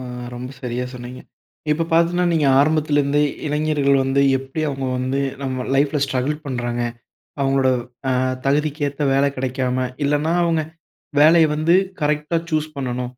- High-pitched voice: No, medium, 140 Hz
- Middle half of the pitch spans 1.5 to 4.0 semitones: Yes, narrow, 2.6 semitones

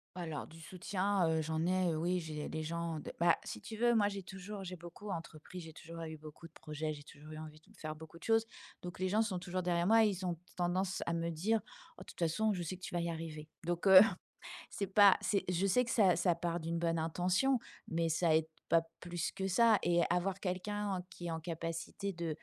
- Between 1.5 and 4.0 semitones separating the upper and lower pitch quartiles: Yes, average, 2.8 semitones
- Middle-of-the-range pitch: Yes, medium, 175 Hz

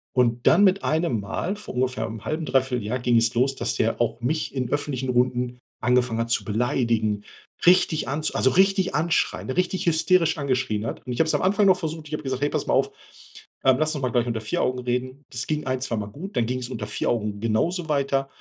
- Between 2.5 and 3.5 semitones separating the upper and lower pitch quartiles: No, average, 4.7 semitones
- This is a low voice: Yes, low, 130 Hz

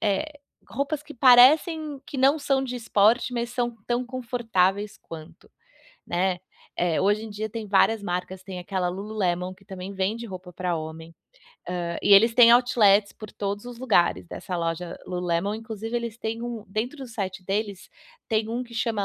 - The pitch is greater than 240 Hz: No, high, 215 Hz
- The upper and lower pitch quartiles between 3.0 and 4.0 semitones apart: No, average, 4.4 semitones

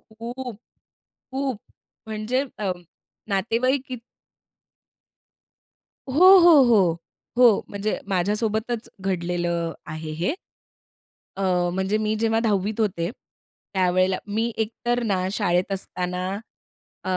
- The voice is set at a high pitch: Yes, high, 210 Hz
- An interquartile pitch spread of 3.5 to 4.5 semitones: Yes, average, 4.0 semitones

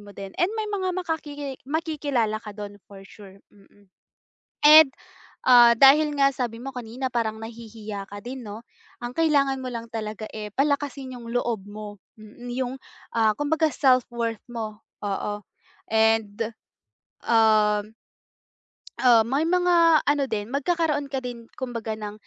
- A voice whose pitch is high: Yes, high, 240 Hz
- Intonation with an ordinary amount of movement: Yes, average, 4.7 semitones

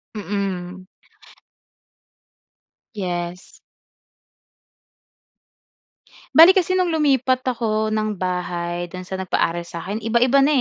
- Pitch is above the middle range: Yes, high, 205 Hz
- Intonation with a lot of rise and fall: Yes, wide, 6.1 semitones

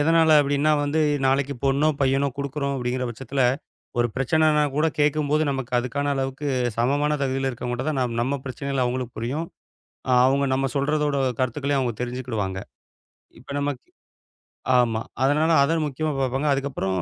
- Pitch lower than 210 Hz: Yes, low, 135 Hz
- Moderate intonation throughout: No, narrow, 2.3 semitones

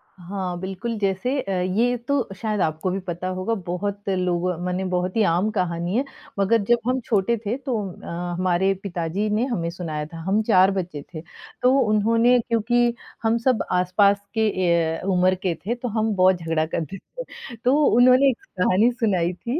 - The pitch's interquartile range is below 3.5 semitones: No, average, 4.3 semitones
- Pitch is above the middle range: Yes, high, 195 Hz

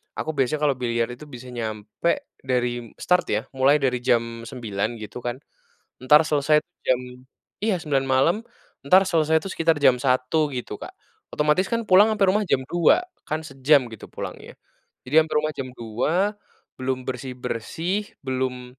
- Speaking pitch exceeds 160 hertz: No, low, 130 Hz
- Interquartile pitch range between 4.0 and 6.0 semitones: Yes, average, 4.5 semitones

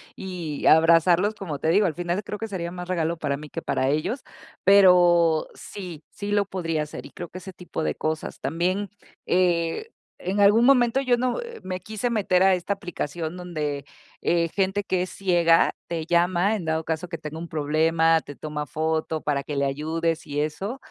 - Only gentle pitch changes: No, average, 3.4 semitones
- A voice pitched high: No, medium, 175 Hz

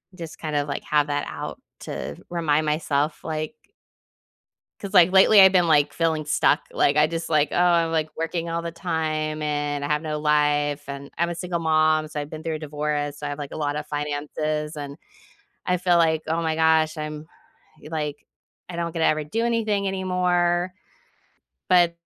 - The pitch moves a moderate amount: No, narrow, 2.2 semitones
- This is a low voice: No, medium, 155 Hz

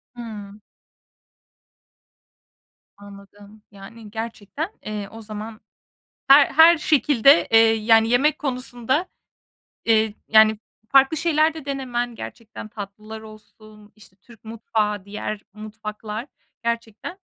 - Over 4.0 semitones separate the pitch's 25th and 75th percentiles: No, average, 3.0 semitones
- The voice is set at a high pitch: Yes, high, 220 Hz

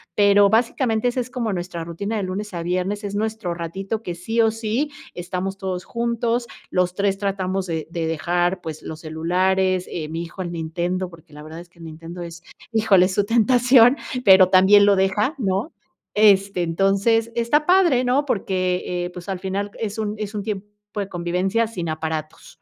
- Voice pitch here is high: Yes, high, 195 Hz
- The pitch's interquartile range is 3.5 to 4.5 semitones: Yes, average, 3.9 semitones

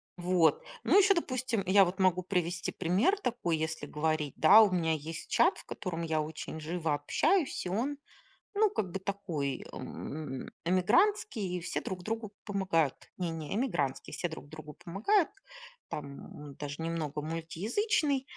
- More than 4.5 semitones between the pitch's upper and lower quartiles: Yes, wide, 5.5 semitones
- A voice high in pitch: No, medium, 180 Hz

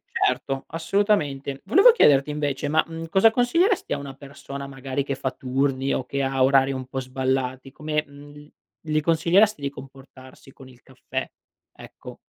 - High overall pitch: No, medium, 140 Hz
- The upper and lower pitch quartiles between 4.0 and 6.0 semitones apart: No, average, 2.8 semitones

